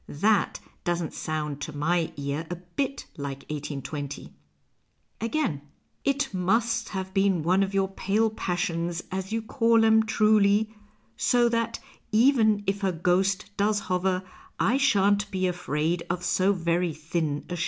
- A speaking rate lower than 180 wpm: Yes, average, 150 wpm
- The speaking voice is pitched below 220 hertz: Yes, high, 190 Hz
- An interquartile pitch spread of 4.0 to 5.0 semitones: Yes, average, 4.3 semitones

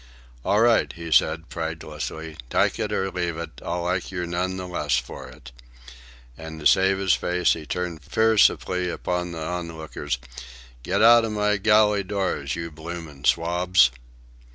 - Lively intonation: No, average, 2.9 semitones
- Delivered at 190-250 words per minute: No, average, 155 wpm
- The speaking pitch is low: Yes, very low, 85 Hz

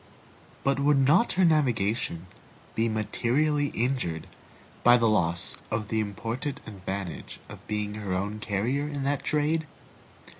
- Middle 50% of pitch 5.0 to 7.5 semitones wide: Yes, wide, 5.6 semitones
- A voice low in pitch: Yes, low, 115 Hz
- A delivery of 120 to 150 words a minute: Yes, slow, 135 wpm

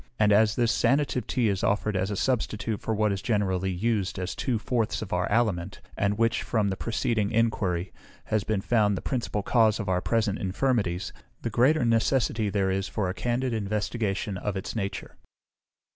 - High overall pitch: No, low, 105 Hz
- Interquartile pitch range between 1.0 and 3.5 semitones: Yes, average, 2.9 semitones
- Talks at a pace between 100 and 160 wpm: No, average, 185 wpm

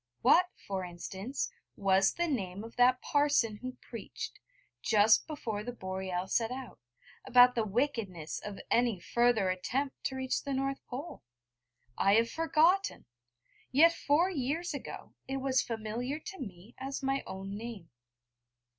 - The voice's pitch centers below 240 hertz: No, high, 245 Hz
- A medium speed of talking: Yes, average, 145 wpm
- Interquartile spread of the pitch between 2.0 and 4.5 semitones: No, average, 5.3 semitones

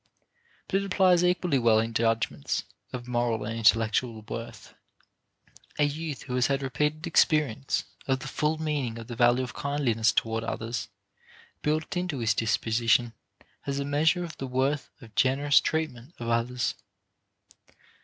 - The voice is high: No, low, 130 Hz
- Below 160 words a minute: Yes, average, 150 wpm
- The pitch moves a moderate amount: Yes, average, 4.5 semitones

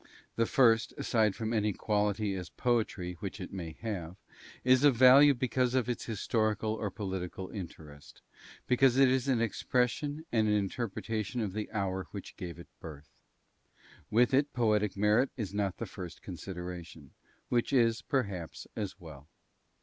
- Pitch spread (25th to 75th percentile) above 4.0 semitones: Yes, average, 4.5 semitones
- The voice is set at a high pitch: No, low, 105 Hz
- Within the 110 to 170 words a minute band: Yes, average, 155 wpm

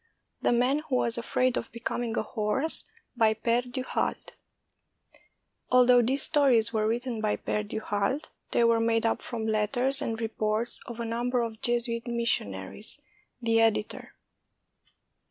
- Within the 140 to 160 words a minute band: Yes, average, 150 wpm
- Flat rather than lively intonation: Yes, narrow, 2.0 semitones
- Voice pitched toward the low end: No, high, 235 Hz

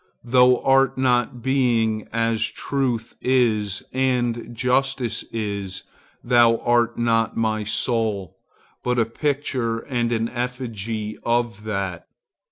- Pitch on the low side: Yes, low, 120 Hz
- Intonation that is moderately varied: No, narrow, 2.3 semitones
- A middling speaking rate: No, slow, 100 wpm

